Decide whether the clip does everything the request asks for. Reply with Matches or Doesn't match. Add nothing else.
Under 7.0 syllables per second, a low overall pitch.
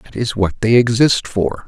Matches